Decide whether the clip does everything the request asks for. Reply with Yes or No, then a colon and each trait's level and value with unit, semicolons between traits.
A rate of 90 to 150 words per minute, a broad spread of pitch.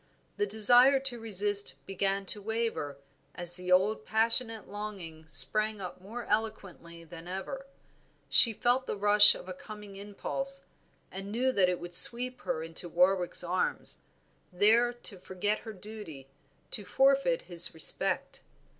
No: average, 140 wpm; average, 3.9 semitones